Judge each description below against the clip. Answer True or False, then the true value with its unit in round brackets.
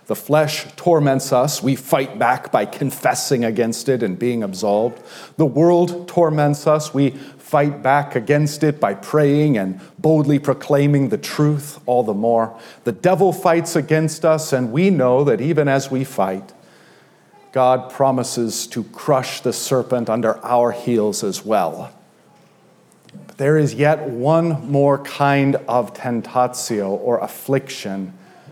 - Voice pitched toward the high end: False (140 Hz)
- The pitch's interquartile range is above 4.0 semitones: False (3.7 semitones)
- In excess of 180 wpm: False (145 wpm)